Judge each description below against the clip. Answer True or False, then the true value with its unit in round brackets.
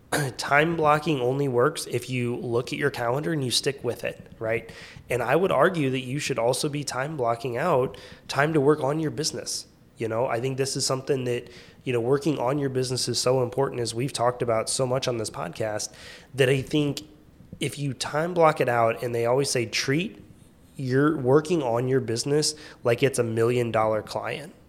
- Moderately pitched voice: False (130 Hz)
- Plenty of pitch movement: False (3.3 semitones)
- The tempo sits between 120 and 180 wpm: False (205 wpm)